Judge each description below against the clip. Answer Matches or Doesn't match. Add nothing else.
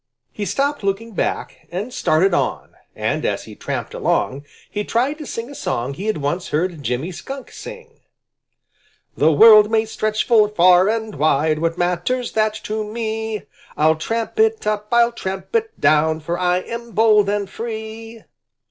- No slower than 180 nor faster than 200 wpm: Doesn't match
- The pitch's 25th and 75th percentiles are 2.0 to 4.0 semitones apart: Doesn't match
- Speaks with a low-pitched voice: Doesn't match